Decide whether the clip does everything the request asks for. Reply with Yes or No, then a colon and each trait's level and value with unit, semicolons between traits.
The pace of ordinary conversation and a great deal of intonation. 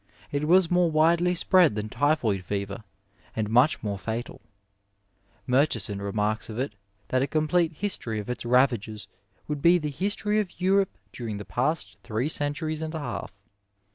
Yes: average, 160 wpm; wide, 7.0 semitones